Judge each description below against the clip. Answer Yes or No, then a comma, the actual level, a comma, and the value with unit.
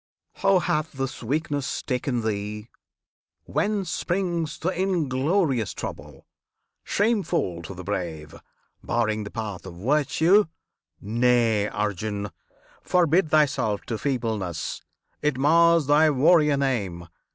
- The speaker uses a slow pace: Yes, slow, 105 wpm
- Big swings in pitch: Yes, wide, 7.2 semitones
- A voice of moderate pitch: No, low, 130 Hz